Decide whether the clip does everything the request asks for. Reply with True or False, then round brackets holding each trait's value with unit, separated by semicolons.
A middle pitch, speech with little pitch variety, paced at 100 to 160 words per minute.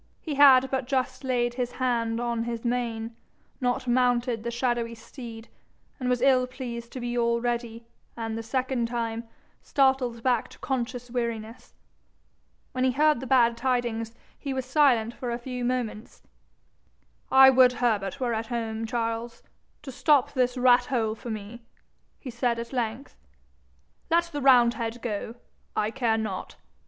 False (240 Hz; 1.8 semitones; 155 wpm)